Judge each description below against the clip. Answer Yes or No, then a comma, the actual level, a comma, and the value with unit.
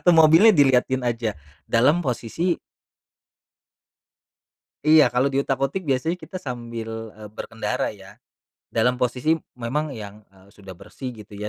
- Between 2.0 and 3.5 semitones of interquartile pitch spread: No, average, 4.7 semitones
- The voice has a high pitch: No, low, 125 Hz